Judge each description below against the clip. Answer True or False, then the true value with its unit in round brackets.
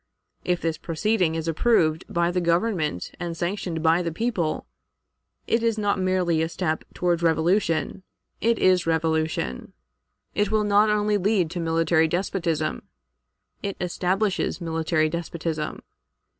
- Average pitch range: True (3.4 semitones)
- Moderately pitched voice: True (170 Hz)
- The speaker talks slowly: True (130 wpm)